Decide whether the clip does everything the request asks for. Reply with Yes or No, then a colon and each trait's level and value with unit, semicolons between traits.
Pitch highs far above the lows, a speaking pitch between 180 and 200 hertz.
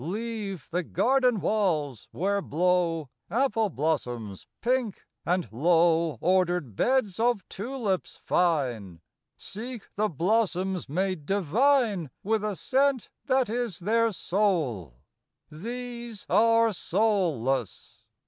Yes: wide, 5.9 semitones; high, 190 Hz